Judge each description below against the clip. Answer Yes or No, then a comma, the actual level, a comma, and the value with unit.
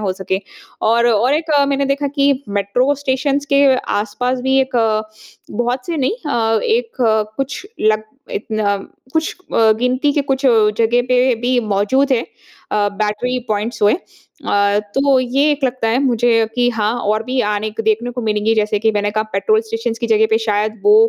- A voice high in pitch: Yes, high, 235 Hz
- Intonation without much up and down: No, average, 3.6 semitones